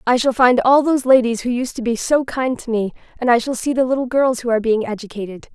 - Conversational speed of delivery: No, fast, 270 wpm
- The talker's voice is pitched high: Yes, high, 245 Hz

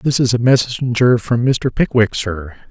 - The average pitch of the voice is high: No, low, 120 Hz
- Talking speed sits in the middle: Yes, average, 175 wpm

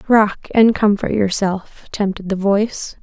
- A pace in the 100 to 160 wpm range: Yes, average, 140 wpm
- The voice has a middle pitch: No, high, 205 Hz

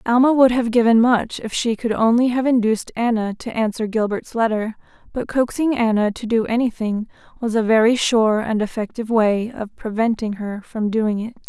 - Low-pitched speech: No, high, 225 Hz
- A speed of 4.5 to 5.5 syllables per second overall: Yes, 5.3 syllables/s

